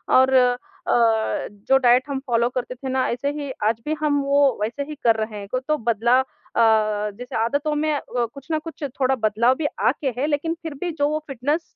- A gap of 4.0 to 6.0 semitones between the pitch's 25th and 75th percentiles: No, average, 3.4 semitones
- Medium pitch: No, very high, 260 Hz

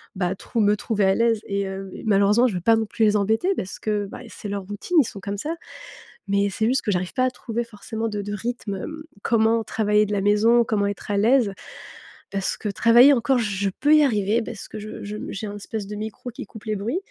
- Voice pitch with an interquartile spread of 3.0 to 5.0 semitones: No, narrow, 2.4 semitones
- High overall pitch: Yes, high, 210 Hz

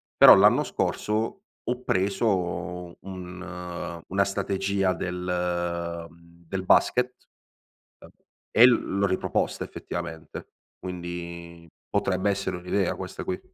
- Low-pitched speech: Yes, very low, 90 Hz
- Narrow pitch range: Yes, narrow, 2.2 semitones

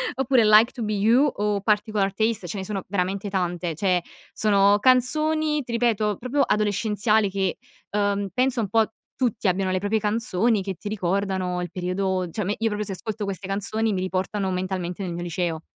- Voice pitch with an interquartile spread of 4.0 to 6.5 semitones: No, average, 2.8 semitones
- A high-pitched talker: Yes, high, 205 Hz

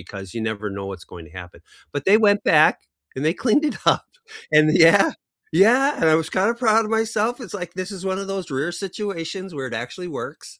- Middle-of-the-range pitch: Yes, medium, 180 Hz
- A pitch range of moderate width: No, wide, 7.3 semitones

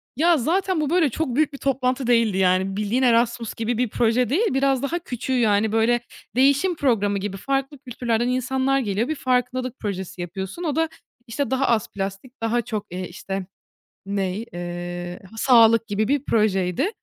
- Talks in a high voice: Yes, high, 240 Hz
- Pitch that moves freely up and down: No, average, 5.0 semitones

